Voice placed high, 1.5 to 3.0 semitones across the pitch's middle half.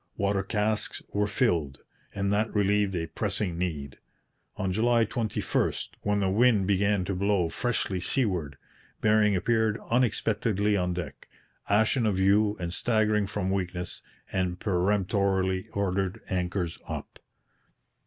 No: low, 100 Hz; narrow, 2.6 semitones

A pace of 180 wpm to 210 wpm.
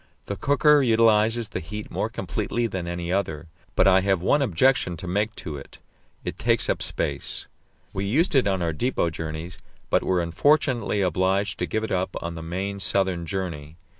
Yes: average, 185 wpm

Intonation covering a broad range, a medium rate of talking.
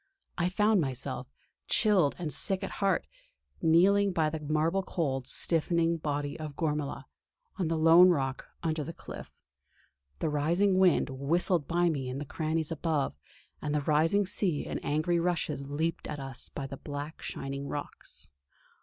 No: average, 3.4 semitones; average, 155 wpm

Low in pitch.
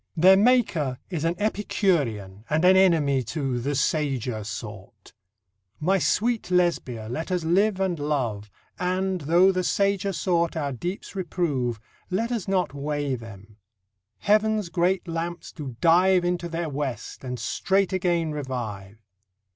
No: medium, 165 Hz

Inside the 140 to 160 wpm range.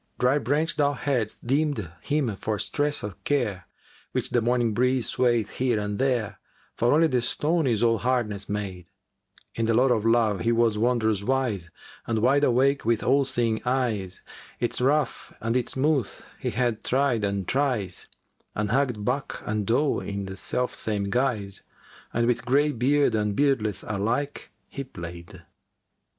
No: average, 170 wpm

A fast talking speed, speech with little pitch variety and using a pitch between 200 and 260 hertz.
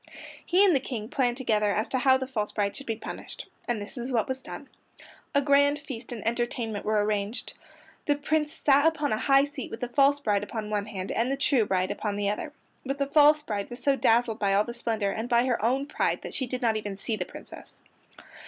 No: fast, 235 wpm; average, 4.5 semitones; high, 240 Hz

